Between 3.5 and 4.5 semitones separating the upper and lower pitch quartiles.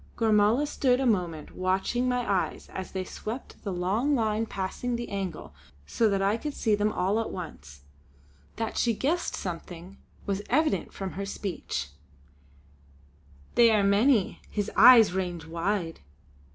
Yes: average, 4.0 semitones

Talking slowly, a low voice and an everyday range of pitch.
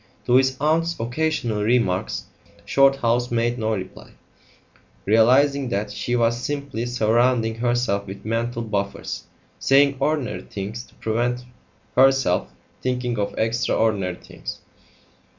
Yes: slow, 115 wpm; low, 120 Hz; average, 3.1 semitones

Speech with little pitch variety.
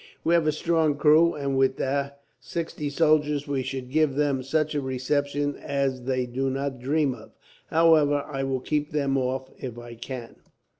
Yes: narrow, 2.2 semitones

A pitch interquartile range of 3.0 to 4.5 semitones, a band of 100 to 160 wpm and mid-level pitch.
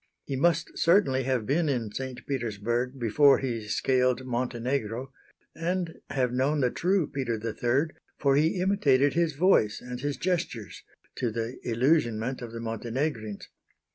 No: average, 4.0 semitones; average, 140 wpm; low, 130 Hz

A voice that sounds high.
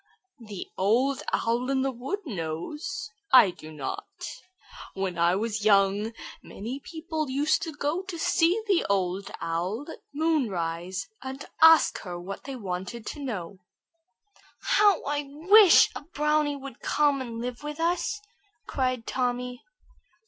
Yes: very high, 255 Hz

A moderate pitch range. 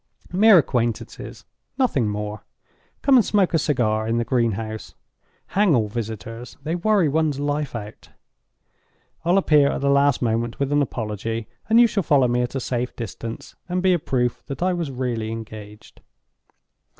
No: wide, 6.0 semitones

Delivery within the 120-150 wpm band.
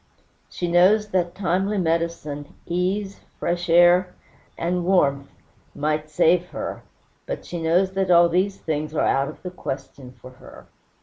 Yes: average, 145 wpm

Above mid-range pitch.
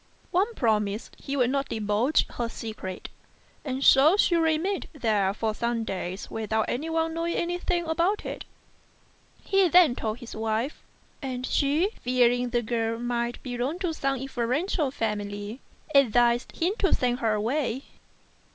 Yes: high, 245 Hz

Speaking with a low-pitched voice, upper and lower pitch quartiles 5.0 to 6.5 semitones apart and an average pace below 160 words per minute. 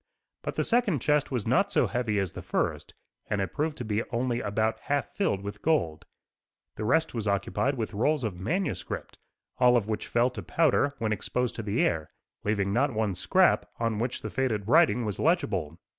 No: low, 115 Hz; wide, 5.6 semitones; average, 195 wpm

